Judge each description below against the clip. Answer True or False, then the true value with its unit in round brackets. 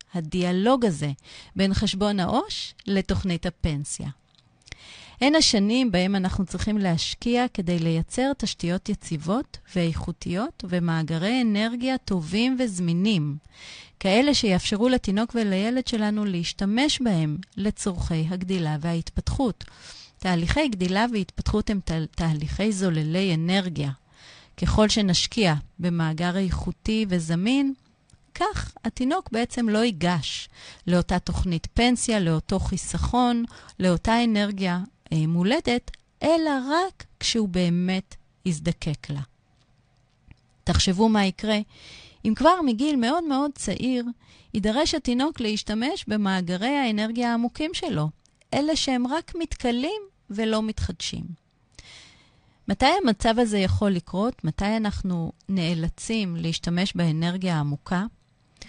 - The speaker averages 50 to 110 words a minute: True (100 wpm)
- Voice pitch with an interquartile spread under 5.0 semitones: False (5.5 semitones)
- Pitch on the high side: True (200 Hz)